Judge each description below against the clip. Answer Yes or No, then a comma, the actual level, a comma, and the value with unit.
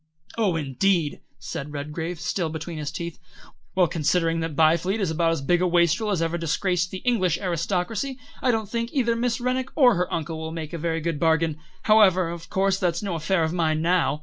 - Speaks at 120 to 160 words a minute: No, average, 200 wpm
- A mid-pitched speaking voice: Yes, medium, 170 Hz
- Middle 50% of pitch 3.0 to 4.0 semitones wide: Yes, average, 3.3 semitones